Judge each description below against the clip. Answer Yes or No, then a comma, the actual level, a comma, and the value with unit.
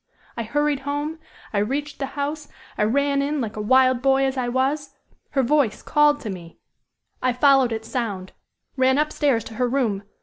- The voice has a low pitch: No, very high, 265 Hz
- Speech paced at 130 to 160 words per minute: No, average, 180 wpm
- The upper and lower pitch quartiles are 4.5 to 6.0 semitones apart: No, average, 3.6 semitones